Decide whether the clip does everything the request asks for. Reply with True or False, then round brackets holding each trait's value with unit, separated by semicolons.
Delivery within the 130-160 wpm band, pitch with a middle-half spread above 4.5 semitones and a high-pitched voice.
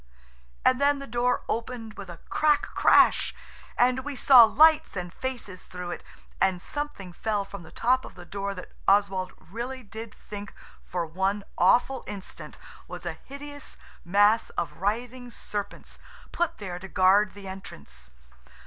True (155 wpm; 5.0 semitones; 205 Hz)